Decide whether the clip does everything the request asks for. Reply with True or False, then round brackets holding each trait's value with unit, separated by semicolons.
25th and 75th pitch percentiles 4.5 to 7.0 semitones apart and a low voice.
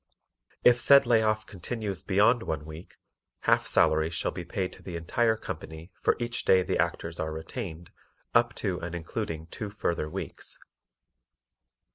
True (5.4 semitones; 95 Hz)